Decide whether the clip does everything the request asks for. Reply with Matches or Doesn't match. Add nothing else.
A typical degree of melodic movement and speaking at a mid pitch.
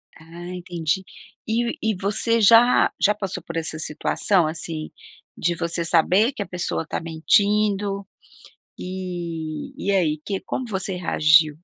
Matches